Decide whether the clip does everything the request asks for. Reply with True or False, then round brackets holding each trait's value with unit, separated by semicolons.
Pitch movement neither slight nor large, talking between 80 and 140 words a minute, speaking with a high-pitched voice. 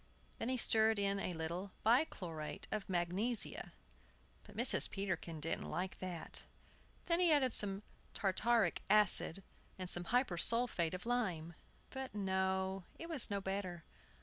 True (4.6 semitones; 135 wpm; 195 Hz)